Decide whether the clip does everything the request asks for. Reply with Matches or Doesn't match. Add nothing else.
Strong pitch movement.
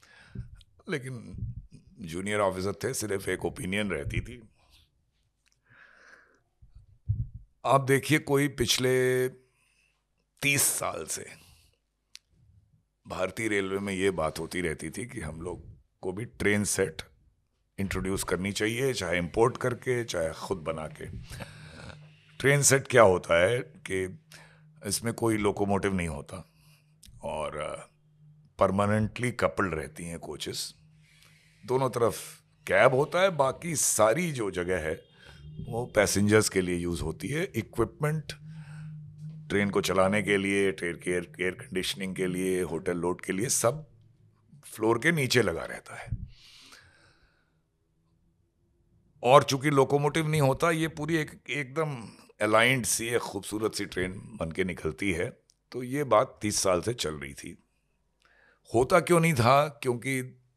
Matches